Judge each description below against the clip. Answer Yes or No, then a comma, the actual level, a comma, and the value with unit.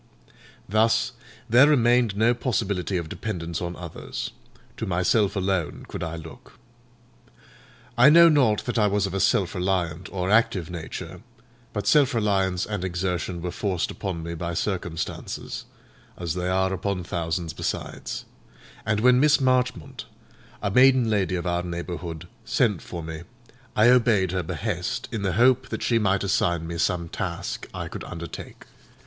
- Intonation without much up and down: No, average, 4.6 semitones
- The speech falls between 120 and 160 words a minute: Yes, average, 155 wpm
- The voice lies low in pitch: Yes, very low, 95 Hz